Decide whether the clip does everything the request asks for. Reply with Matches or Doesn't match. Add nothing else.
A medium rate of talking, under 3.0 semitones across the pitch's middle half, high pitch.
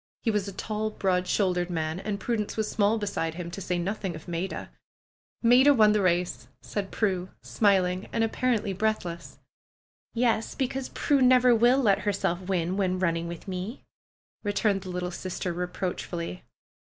Doesn't match